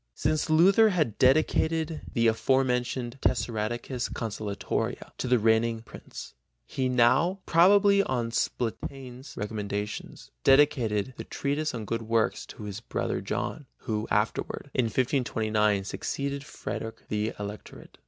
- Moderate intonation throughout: Yes, average, 4.2 semitones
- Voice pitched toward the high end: No, low, 120 Hz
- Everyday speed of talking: No, slow, 125 wpm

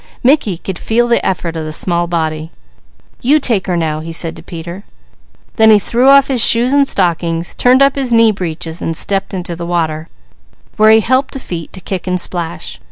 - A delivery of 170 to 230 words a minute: Yes, fast, 205 wpm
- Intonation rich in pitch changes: Yes, wide, 6.0 semitones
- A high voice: No, medium, 180 Hz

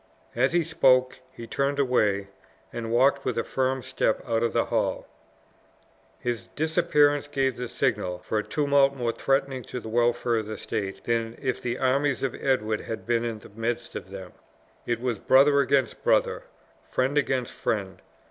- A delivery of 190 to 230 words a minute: No, average, 175 wpm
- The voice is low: Yes, low, 125 Hz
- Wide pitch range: No, average, 3.2 semitones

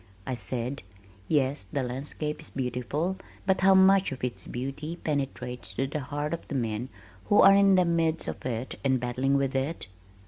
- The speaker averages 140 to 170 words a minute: No, average, 180 wpm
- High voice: No, low, 135 Hz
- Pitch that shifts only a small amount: No, average, 4.6 semitones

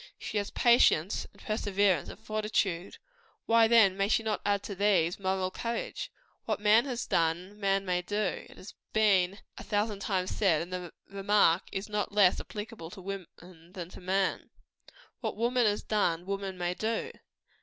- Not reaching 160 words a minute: No, average, 165 wpm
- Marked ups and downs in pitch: No, average, 2.7 semitones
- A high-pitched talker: Yes, high, 195 Hz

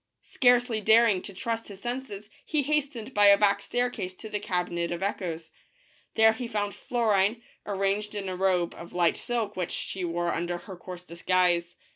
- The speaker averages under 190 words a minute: No, average, 195 wpm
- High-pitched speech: Yes, high, 200 Hz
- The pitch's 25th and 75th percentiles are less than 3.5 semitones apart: No, average, 4.0 semitones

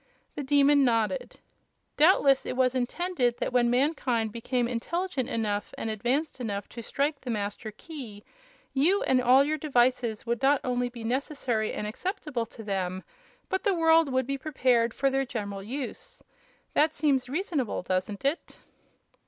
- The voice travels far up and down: No, average, 4.1 semitones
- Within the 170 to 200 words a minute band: No, average, 155 wpm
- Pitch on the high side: Yes, very high, 255 Hz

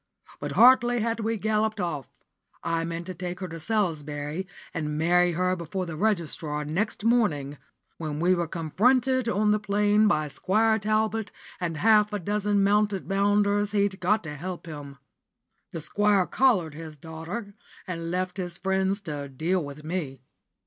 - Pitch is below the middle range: No, medium, 185 Hz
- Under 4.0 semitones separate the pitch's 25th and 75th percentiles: No, average, 4.5 semitones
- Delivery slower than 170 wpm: Yes, average, 160 wpm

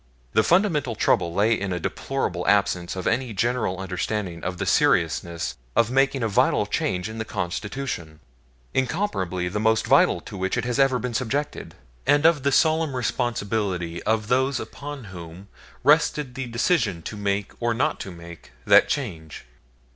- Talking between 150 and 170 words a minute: Yes, average, 160 wpm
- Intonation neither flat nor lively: No, wide, 6.4 semitones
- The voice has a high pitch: No, low, 110 Hz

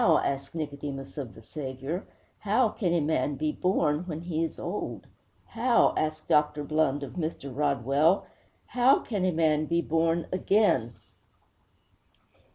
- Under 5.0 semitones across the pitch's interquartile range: Yes, average, 3.5 semitones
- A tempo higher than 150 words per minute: No, average, 145 wpm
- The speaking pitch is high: No, medium, 155 Hz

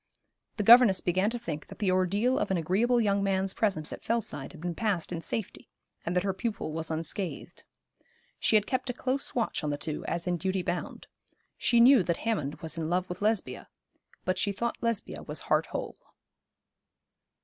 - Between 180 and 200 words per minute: Yes, average, 195 wpm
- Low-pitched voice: No, high, 190 Hz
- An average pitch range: Yes, average, 4.9 semitones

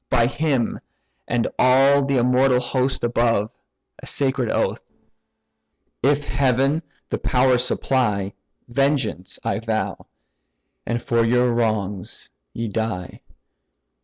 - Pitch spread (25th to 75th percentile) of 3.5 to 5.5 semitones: No, average, 2.8 semitones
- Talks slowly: Yes, slow, 105 wpm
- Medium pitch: No, low, 125 Hz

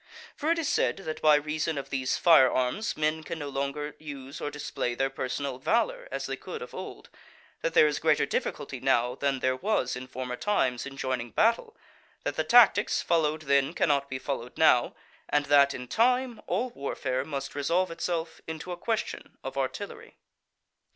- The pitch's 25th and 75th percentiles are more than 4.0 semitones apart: Yes, average, 4.5 semitones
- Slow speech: No, average, 185 wpm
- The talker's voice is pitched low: No, medium, 145 Hz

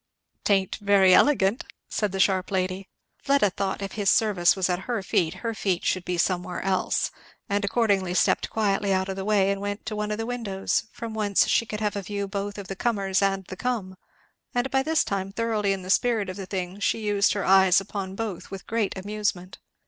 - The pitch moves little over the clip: Yes, narrow, 1.9 semitones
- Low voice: No, high, 200 Hz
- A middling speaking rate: No, fast, 215 wpm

